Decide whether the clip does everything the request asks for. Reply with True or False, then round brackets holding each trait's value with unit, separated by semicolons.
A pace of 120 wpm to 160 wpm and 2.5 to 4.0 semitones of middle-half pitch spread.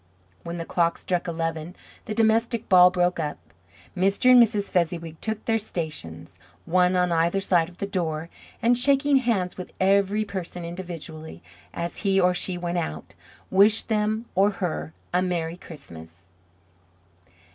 True (150 wpm; 3.6 semitones)